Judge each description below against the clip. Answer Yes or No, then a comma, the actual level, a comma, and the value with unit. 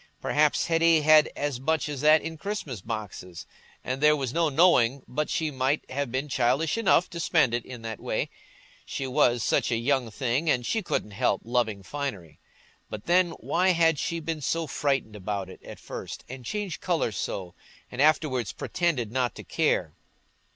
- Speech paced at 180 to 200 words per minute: Yes, average, 185 wpm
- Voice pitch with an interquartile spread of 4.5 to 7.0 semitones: Yes, average, 5.2 semitones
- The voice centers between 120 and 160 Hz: Yes, medium, 140 Hz